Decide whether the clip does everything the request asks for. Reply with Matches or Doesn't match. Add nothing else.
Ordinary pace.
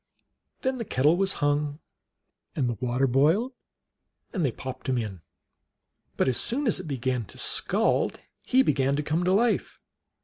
Matches